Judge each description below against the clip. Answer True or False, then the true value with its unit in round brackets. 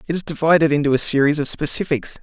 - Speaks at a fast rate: True (215 wpm)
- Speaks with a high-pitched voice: False (150 Hz)